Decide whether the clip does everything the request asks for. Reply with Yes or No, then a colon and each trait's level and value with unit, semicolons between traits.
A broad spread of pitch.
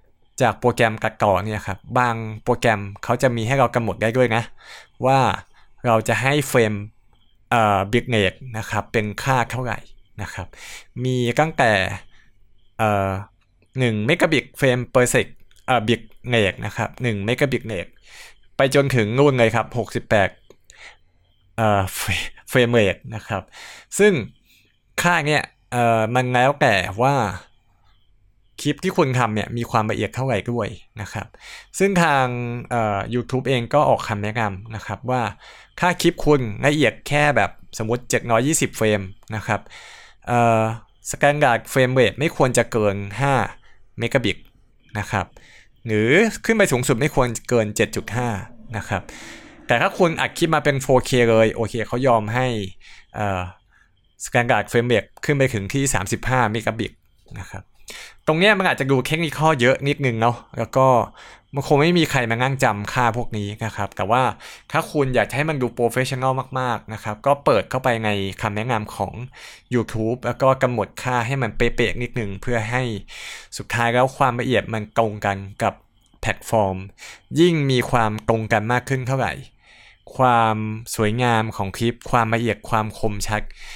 No: average, 3.5 semitones